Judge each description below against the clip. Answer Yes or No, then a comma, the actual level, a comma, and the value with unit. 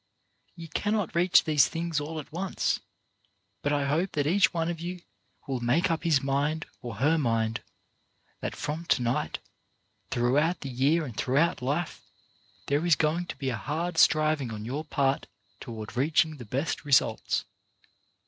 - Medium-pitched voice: Yes, medium, 150 Hz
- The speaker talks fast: No, average, 165 wpm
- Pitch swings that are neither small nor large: Yes, average, 4.1 semitones